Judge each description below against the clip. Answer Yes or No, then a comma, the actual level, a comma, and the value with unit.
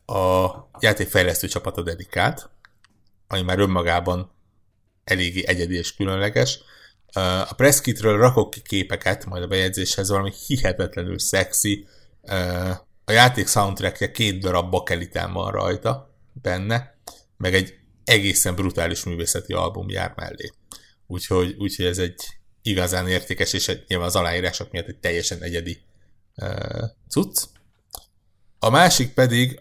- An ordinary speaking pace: Yes, average, 120 wpm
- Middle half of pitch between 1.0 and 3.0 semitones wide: Yes, narrow, 2.6 semitones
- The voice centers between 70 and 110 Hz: Yes, very low, 95 Hz